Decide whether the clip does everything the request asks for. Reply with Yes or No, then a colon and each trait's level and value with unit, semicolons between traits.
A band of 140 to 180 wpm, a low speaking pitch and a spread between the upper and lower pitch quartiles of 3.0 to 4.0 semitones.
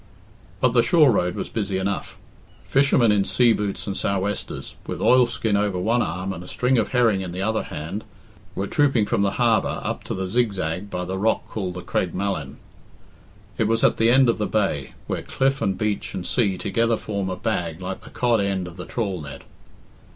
No: fast, 205 wpm; low, 100 Hz; average, 3.6 semitones